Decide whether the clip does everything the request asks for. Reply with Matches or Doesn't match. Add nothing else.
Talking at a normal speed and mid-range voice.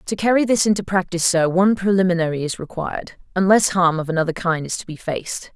Matches